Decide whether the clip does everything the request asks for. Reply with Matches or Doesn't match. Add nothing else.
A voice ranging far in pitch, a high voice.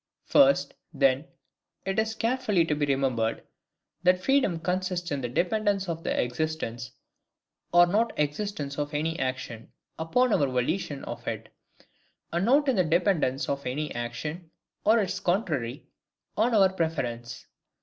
Doesn't match